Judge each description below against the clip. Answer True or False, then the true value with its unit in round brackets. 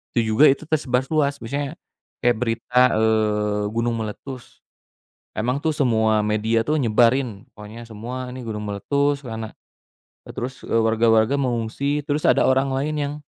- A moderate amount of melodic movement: True (3.8 semitones)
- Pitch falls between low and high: False (120 Hz)